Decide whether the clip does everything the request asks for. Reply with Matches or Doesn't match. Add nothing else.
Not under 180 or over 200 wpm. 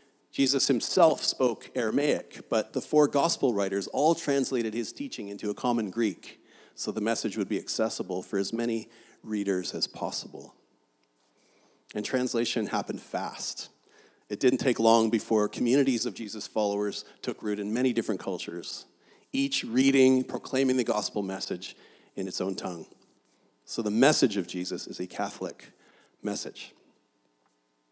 Doesn't match